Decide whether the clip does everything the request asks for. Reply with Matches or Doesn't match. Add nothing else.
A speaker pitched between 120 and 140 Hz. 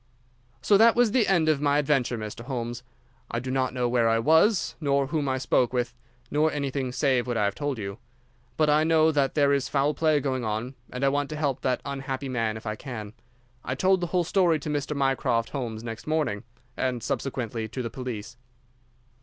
Matches